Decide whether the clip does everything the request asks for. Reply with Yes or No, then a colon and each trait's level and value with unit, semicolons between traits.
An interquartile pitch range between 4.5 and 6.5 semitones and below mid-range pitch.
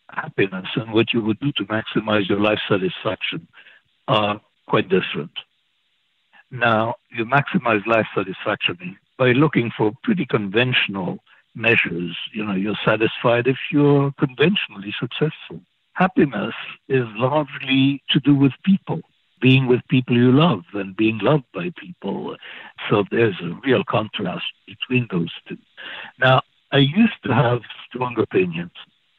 Yes: average, 4.8 semitones; low, 125 Hz